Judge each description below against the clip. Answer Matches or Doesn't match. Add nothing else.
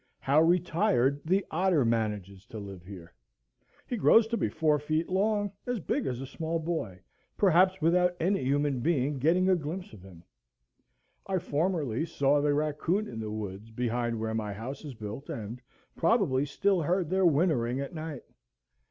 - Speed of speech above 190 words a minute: Doesn't match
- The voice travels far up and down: Matches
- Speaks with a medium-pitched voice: Matches